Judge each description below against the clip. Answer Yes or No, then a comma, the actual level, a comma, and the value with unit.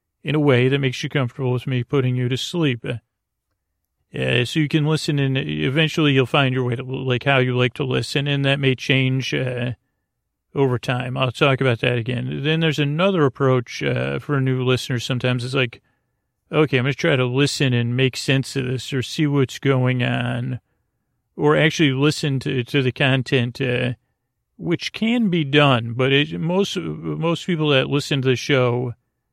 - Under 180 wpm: No, average, 190 wpm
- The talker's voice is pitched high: No, low, 130 Hz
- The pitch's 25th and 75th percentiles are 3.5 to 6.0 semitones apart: No, average, 2.7 semitones